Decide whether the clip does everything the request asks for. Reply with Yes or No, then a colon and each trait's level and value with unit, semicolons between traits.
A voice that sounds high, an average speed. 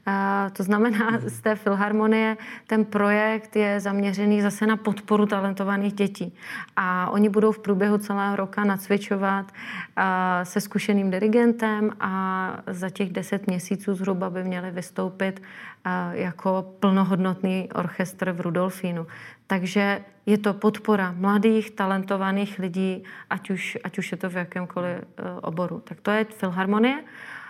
Yes: high, 200 Hz; average, 130 wpm